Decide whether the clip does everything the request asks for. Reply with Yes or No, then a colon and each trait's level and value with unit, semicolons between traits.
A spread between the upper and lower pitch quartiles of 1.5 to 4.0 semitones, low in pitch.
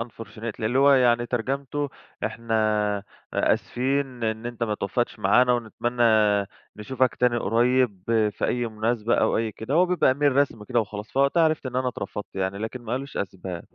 Yes: average, 3.0 semitones; low, 120 Hz